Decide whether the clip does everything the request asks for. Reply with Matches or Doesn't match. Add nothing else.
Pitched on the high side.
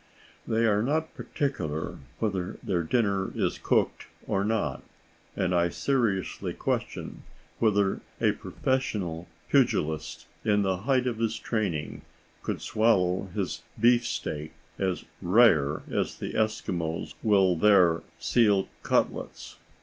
Doesn't match